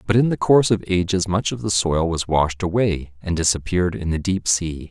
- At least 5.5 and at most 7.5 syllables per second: No, 5.3 syllables/s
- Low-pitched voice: Yes, very low, 90 Hz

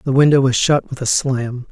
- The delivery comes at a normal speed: No, fast, 245 wpm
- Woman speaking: No, male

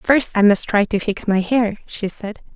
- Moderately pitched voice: No, high, 215 Hz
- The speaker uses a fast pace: Yes, fast, 235 wpm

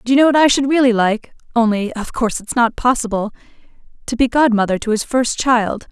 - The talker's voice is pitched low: No, high, 235 Hz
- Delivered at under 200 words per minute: No, fast, 205 wpm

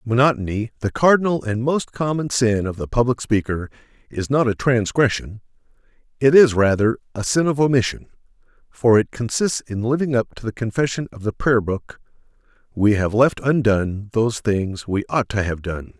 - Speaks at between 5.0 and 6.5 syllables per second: Yes, 5.1 syllables/s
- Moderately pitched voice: No, low, 115 Hz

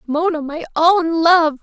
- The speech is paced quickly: No, average, 150 wpm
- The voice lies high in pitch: Yes, very high, 325 Hz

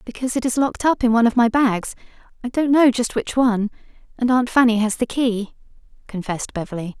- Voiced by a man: No, female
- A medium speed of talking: Yes, average, 190 wpm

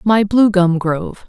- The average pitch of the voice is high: Yes, high, 195 Hz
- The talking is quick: No, average, 190 wpm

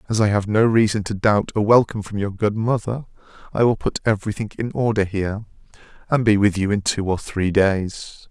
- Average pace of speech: No, fast, 215 wpm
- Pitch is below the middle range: Yes, low, 105 Hz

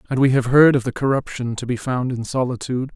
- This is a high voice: No, low, 125 Hz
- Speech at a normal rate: No, fast, 245 wpm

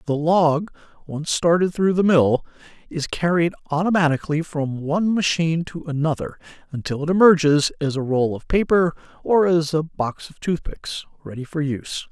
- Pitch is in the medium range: Yes, medium, 160 Hz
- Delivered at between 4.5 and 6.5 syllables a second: Yes, 5.1 syllables/s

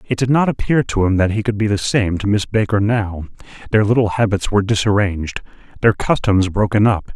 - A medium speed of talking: No, fast, 210 wpm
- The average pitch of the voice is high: No, low, 105 Hz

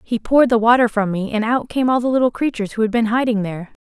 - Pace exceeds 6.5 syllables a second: Yes, 6.9 syllables/s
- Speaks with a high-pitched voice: Yes, high, 230 Hz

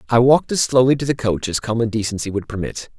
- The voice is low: Yes, low, 115 Hz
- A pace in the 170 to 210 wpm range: No, fast, 240 wpm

